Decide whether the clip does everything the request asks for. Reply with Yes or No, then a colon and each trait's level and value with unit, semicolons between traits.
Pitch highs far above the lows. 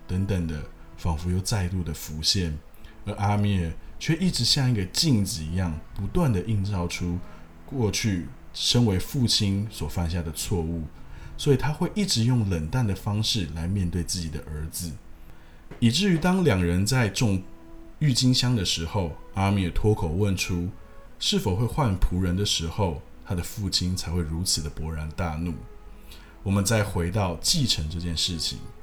No: average, 4.8 semitones